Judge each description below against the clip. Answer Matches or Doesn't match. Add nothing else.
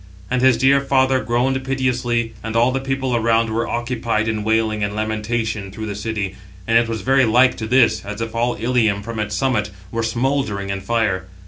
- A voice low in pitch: Matches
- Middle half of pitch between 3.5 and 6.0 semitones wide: Doesn't match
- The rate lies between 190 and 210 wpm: Matches